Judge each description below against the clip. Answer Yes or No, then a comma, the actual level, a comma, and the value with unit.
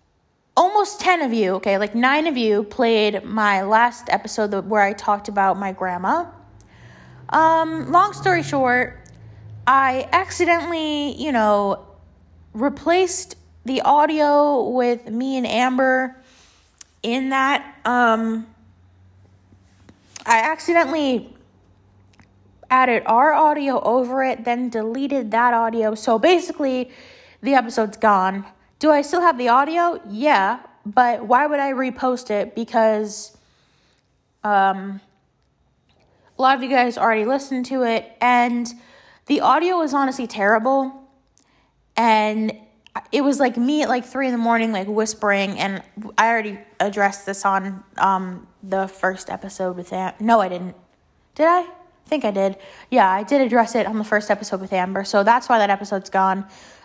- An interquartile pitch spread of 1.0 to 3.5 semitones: No, average, 5.3 semitones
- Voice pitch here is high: Yes, high, 230 Hz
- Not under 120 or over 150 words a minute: Yes, average, 140 wpm